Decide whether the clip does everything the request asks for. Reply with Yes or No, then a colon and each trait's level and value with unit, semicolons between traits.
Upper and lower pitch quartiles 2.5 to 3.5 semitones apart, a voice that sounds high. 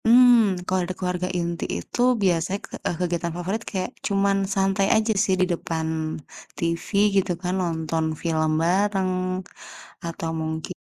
No: average, 2.8 semitones; medium, 180 Hz